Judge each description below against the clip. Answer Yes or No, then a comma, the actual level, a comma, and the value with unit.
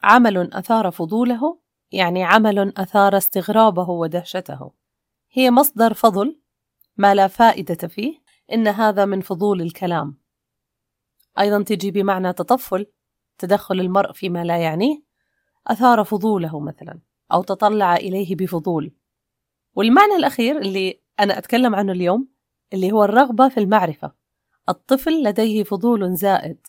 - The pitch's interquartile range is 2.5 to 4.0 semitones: Yes, average, 3.7 semitones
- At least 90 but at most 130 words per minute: Yes, average, 115 wpm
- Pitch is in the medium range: No, high, 200 Hz